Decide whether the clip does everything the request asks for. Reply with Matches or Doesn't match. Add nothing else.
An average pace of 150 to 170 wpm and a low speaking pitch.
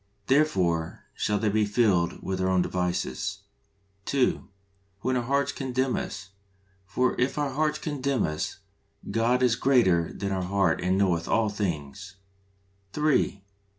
Matches